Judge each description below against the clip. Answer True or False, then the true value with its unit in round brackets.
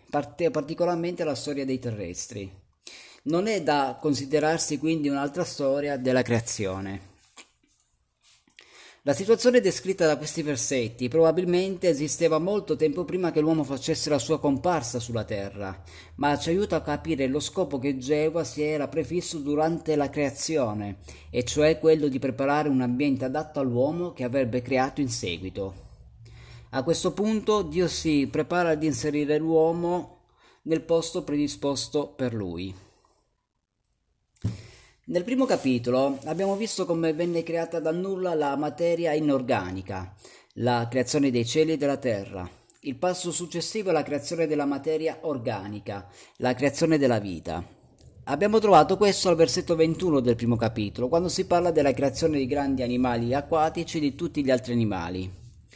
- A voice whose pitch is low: False (145 Hz)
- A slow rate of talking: False (145 wpm)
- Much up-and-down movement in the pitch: False (5.0 semitones)